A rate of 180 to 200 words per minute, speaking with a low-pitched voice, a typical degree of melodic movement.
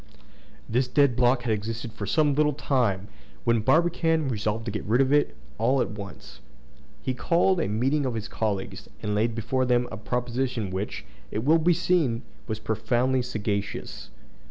No: average, 170 wpm; low, 120 Hz; average, 3.9 semitones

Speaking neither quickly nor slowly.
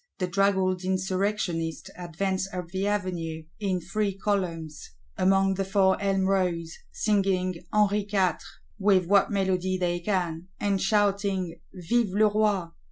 No: slow, 130 wpm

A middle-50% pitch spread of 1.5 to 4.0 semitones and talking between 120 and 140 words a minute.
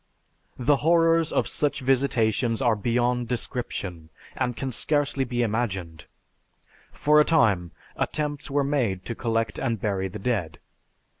No: average, 4.6 semitones; slow, 135 wpm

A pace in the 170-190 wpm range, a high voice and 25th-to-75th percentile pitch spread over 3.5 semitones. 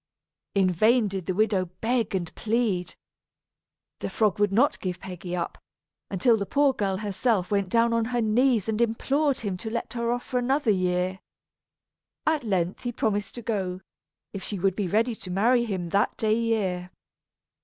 Yes: average, 175 wpm; high, 210 Hz; average, 3.9 semitones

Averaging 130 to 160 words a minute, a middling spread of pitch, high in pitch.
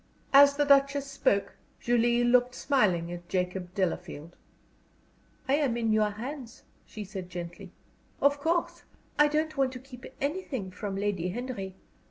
No: average, 145 wpm; wide, 6.6 semitones; high, 235 Hz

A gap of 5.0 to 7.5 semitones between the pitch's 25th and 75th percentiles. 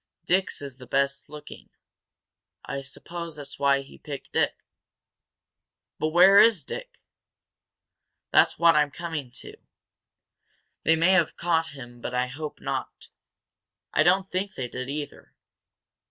No: average, 4.0 semitones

